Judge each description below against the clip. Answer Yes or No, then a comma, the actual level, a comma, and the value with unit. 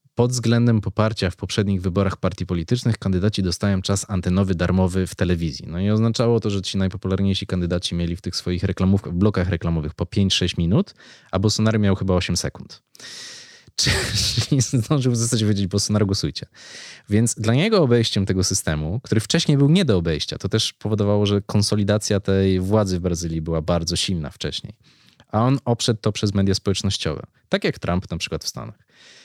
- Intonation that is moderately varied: Yes, average, 3.2 semitones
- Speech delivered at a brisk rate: Yes, fast, 175 wpm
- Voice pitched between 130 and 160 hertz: No, low, 100 Hz